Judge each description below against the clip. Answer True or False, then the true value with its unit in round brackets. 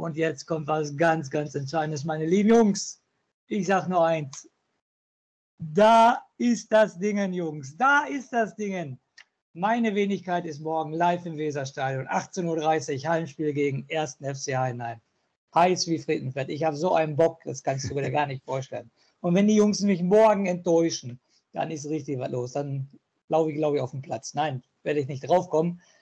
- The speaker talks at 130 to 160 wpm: False (180 wpm)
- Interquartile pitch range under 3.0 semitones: False (4.4 semitones)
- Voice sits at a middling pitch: True (160 Hz)